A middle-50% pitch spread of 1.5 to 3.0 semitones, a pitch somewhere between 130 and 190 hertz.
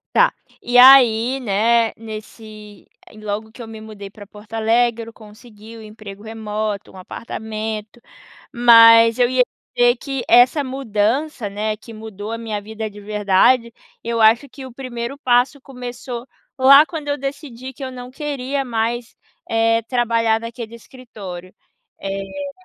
No: average, 2.7 semitones; high, 230 Hz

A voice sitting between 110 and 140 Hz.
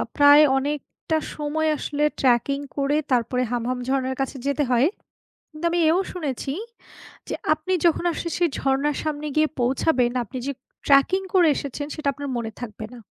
No: very high, 280 Hz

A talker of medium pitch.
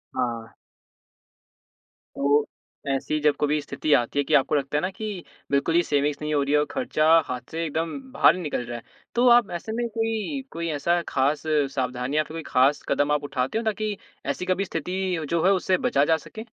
Yes: medium, 155 Hz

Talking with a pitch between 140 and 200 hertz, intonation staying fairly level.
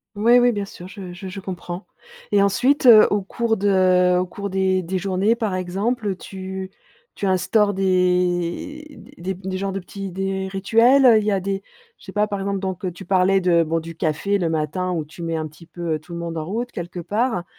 Yes: high, 190 Hz; narrow, 2.3 semitones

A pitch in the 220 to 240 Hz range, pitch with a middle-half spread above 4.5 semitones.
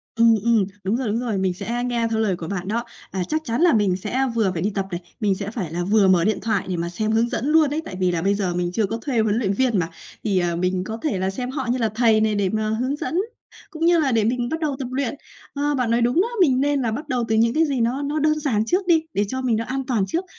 Yes: high, 230 Hz; average, 5.1 semitones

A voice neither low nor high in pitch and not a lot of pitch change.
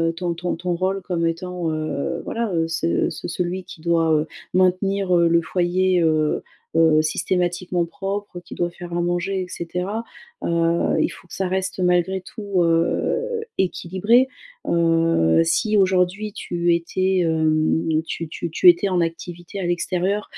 Yes: medium, 175 Hz; narrow, 2.1 semitones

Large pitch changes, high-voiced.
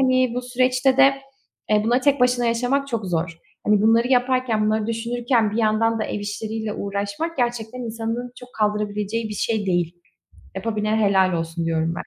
No: average, 3.0 semitones; high, 225 Hz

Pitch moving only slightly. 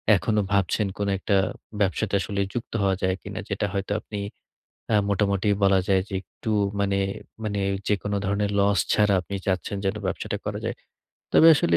Yes: narrow, 1.1 semitones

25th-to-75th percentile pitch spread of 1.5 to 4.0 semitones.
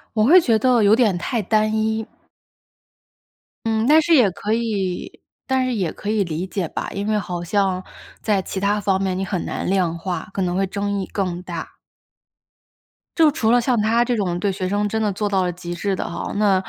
Yes: average, 3.0 semitones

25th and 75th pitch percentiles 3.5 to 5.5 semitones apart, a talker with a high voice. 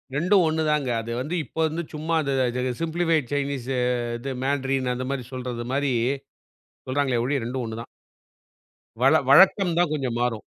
No: average, 3.8 semitones; medium, 140 Hz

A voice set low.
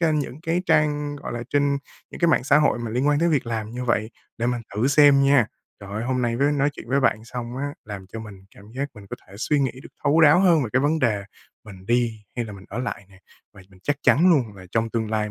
Yes: low, 125 Hz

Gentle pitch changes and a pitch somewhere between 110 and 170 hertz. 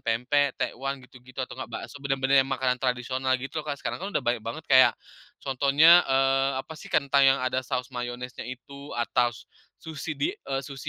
Yes: narrow, 1.8 semitones; low, 135 Hz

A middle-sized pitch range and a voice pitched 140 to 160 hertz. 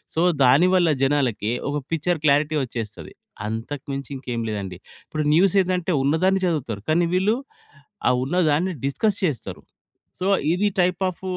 No: wide, 5.7 semitones; medium, 155 Hz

